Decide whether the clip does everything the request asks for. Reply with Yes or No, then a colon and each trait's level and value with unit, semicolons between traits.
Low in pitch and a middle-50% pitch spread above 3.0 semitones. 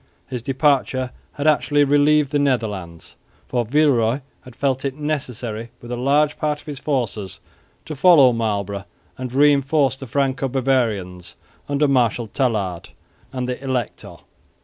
Yes: low, 130 Hz; average, 3.6 semitones